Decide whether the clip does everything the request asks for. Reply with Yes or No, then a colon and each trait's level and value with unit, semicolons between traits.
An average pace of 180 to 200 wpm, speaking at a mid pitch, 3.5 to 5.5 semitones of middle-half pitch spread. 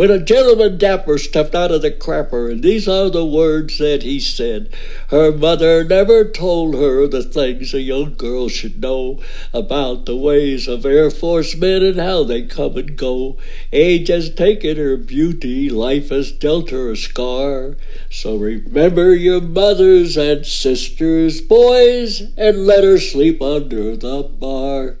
No: average, 160 wpm; medium, 150 Hz; average, 4.8 semitones